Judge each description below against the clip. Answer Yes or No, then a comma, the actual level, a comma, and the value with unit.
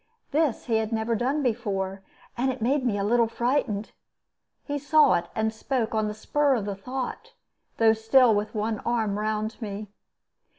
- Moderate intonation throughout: Yes, average, 3.2 semitones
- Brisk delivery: No, average, 175 wpm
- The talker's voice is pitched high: Yes, high, 225 Hz